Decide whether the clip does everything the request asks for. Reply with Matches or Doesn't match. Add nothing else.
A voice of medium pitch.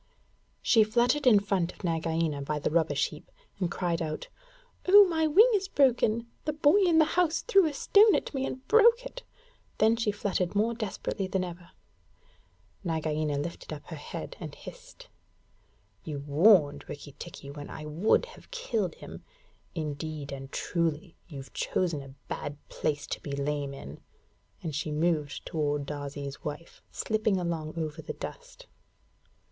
Matches